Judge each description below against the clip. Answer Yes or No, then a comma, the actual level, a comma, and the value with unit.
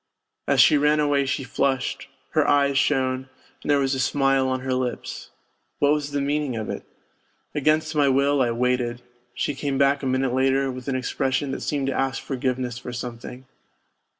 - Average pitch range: No, narrow, 1.8 semitones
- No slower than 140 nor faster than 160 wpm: No, average, 185 wpm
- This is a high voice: No, low, 135 Hz